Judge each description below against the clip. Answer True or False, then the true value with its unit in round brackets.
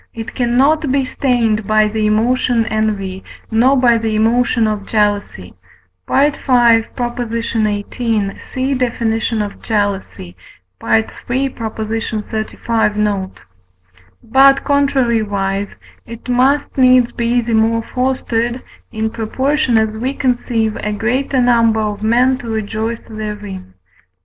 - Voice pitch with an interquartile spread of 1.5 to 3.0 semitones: True (2.7 semitones)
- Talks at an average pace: False (110 wpm)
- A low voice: False (225 Hz)